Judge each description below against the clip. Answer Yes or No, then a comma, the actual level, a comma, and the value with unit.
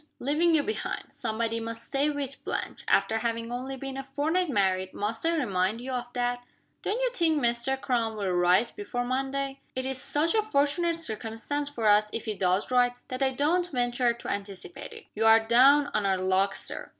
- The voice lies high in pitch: Yes, high, 245 Hz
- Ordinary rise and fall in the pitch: Yes, average, 4.4 semitones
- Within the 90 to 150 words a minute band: No, average, 200 wpm